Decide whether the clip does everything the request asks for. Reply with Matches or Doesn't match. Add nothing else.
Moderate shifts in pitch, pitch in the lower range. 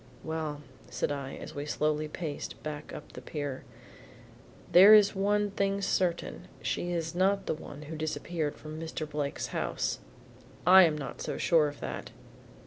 Doesn't match